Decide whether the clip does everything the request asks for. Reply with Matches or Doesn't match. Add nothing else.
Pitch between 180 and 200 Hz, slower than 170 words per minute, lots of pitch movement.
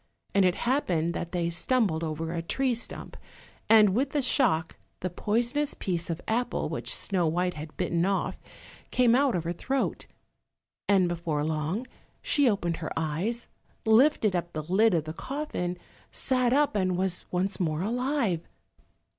Matches